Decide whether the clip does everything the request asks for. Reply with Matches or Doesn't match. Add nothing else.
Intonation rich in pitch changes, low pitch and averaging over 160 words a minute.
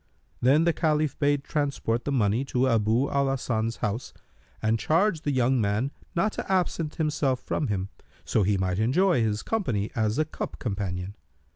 Matches